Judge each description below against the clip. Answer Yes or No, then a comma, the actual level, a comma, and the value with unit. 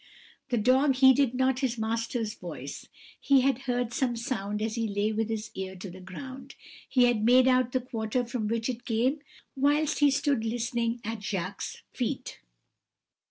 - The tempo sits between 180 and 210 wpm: No, average, 170 wpm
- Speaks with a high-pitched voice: Yes, high, 240 Hz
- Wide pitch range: No, average, 3.0 semitones